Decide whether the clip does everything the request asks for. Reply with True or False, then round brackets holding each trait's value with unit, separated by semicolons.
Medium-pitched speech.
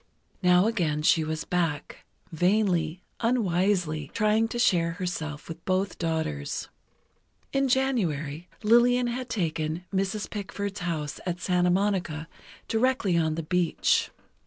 True (180 Hz)